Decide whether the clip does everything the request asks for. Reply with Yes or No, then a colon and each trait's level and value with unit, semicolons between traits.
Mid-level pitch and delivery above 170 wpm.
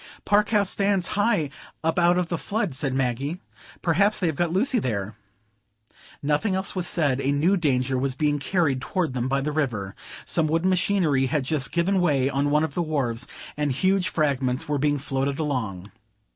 Yes: medium, 150 Hz; average, 185 wpm